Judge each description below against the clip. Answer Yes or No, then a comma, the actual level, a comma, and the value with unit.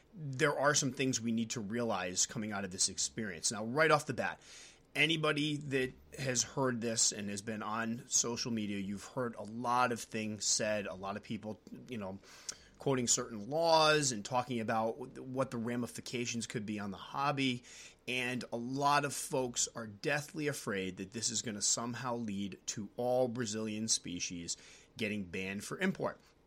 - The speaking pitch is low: Yes, low, 120 Hz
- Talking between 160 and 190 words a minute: Yes, average, 180 wpm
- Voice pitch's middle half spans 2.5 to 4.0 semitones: Yes, average, 3.6 semitones